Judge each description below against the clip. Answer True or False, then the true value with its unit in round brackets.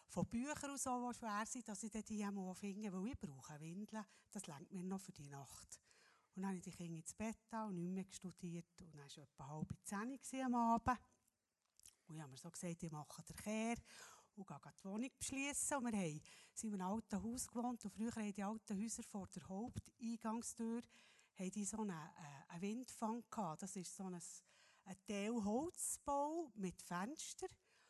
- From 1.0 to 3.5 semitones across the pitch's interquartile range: False (4.5 semitones)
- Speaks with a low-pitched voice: False (200 Hz)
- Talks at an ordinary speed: True (180 wpm)